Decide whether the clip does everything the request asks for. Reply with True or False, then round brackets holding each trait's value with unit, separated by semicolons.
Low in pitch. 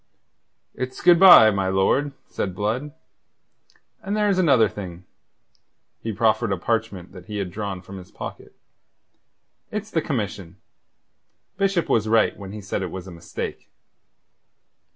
True (110 Hz)